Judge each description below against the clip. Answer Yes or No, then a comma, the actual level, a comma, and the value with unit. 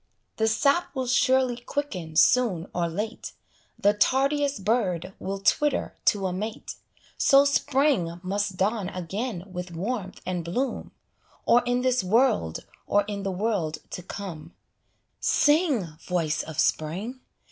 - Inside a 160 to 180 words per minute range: No, slow, 135 wpm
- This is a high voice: Yes, high, 205 Hz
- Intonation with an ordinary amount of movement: No, wide, 5.9 semitones